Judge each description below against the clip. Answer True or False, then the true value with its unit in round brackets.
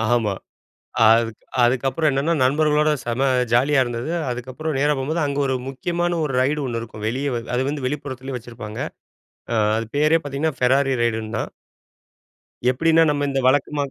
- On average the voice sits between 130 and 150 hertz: True (135 Hz)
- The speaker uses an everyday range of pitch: True (3.6 semitones)